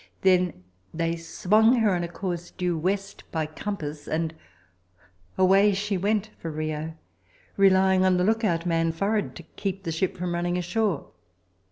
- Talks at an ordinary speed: Yes, average, 155 wpm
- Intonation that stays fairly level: No, average, 3.0 semitones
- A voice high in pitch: No, medium, 180 Hz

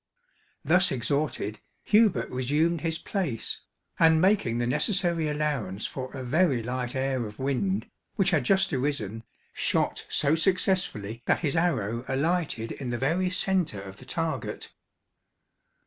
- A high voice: No, medium, 145 Hz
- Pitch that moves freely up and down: Yes, wide, 6.3 semitones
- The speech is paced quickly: No, slow, 135 wpm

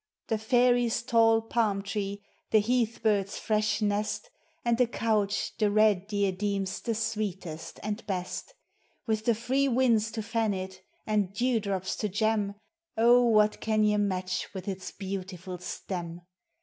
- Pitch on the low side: No, high, 210 Hz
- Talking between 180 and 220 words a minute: No, average, 150 wpm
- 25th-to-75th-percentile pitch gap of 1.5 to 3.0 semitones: Yes, narrow, 2.4 semitones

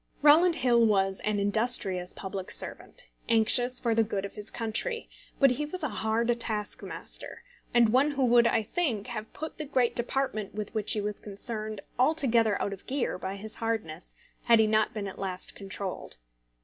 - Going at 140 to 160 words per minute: No, average, 180 wpm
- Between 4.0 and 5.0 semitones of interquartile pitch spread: No, average, 3.2 semitones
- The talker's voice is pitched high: Yes, high, 220 Hz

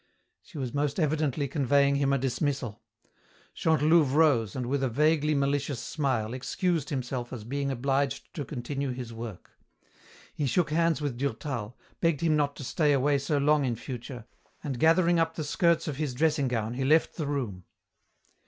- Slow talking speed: No, average, 170 wpm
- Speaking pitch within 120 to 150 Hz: Yes, medium, 140 Hz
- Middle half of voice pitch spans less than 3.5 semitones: Yes, average, 3.1 semitones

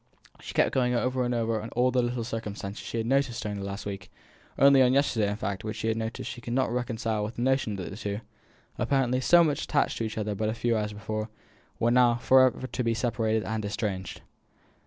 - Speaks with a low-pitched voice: Yes, low, 115 Hz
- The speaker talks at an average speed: No, fast, 220 wpm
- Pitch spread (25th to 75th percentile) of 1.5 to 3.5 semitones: Yes, average, 2.8 semitones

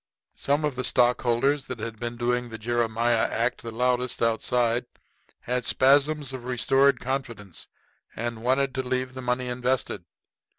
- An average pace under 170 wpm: Yes, average, 145 wpm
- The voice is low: Yes, low, 125 Hz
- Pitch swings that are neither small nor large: No, narrow, 1.8 semitones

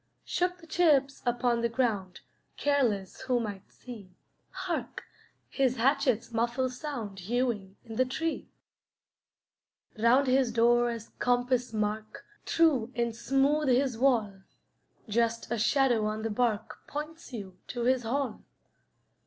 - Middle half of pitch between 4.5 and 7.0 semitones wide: No, average, 3.4 semitones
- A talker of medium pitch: No, high, 240 Hz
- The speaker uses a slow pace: Yes, slow, 130 wpm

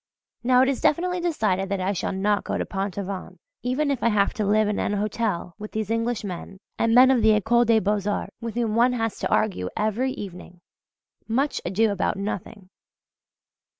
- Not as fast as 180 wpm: No, average, 190 wpm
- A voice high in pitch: Yes, high, 215 Hz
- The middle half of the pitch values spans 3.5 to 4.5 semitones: No, average, 3.1 semitones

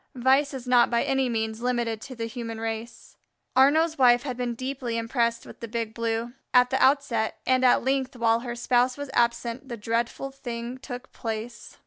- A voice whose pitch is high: Yes, high, 240 Hz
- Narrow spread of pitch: Yes, narrow, 2.1 semitones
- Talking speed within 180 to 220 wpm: Yes, average, 185 wpm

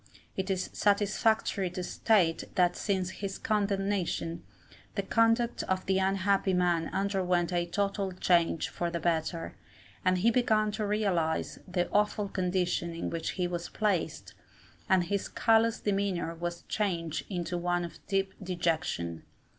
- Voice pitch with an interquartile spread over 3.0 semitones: No, average, 2.7 semitones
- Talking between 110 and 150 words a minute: Yes, average, 140 wpm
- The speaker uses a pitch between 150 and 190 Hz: Yes, medium, 185 Hz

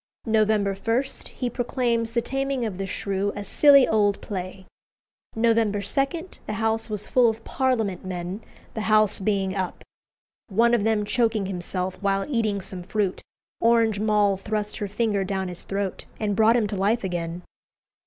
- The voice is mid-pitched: No, high, 210 Hz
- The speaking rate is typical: Yes, average, 165 wpm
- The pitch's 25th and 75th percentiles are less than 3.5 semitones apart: Yes, average, 2.8 semitones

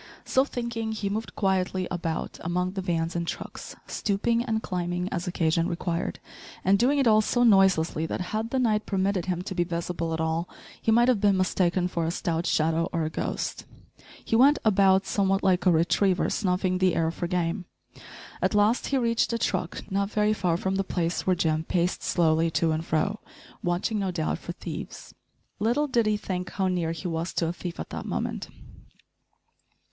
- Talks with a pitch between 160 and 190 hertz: Yes, medium, 185 Hz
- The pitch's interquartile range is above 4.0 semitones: No, average, 3.6 semitones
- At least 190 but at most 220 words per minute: Yes, average, 195 wpm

